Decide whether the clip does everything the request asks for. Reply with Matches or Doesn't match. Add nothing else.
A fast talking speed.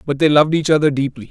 Matches